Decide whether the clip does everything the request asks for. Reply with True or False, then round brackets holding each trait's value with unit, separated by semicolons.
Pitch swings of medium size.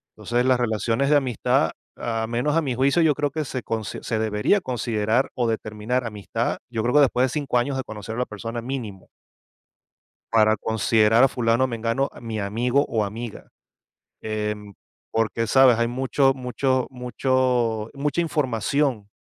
True (3.0 semitones)